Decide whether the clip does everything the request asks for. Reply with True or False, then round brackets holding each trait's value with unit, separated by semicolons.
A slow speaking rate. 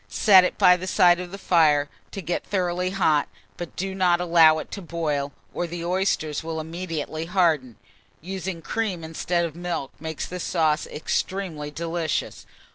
False (165 wpm)